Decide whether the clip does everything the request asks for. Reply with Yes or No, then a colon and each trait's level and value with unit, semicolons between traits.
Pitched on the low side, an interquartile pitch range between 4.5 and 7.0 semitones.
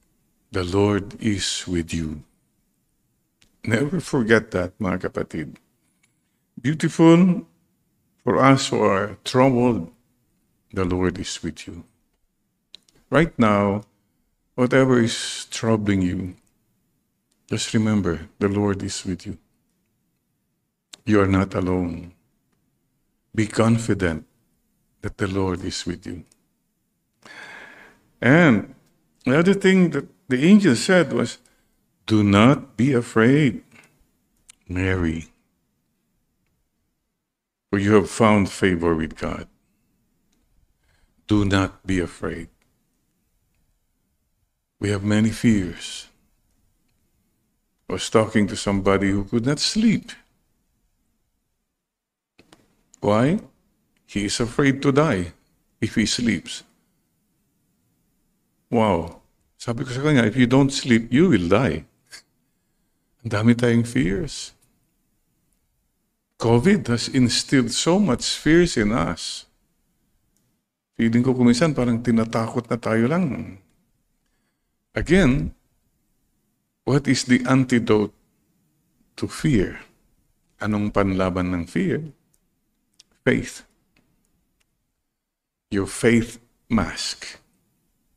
Yes: low, 110 Hz; average, 4.8 semitones